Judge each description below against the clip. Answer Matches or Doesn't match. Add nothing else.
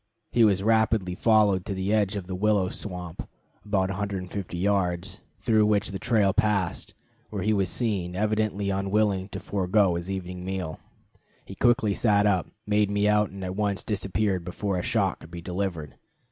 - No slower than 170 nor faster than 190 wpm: Matches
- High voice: Doesn't match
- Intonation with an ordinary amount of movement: Doesn't match